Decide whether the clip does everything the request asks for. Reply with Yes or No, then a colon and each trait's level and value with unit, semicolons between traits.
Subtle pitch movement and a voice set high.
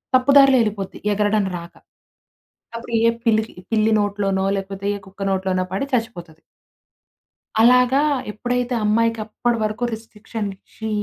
No: average, 3.0 semitones; high, 215 Hz